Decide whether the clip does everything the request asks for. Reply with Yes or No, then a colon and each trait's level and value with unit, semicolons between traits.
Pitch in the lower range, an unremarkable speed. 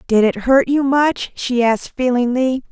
No: very high, 255 Hz; average, 175 wpm